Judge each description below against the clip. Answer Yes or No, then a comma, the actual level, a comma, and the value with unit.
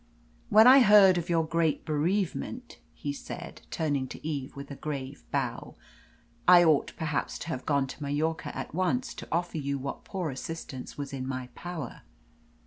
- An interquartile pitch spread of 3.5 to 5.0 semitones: Yes, average, 4.0 semitones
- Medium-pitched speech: Yes, medium, 155 Hz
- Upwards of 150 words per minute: Yes, average, 170 wpm